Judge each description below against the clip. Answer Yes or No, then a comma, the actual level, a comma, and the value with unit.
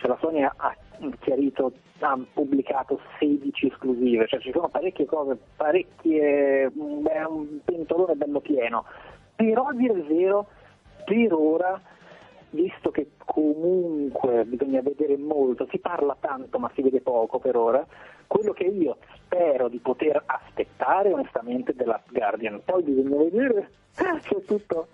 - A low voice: No, medium, 155 Hz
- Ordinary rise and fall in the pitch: No, wide, 5.9 semitones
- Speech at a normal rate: Yes, average, 140 wpm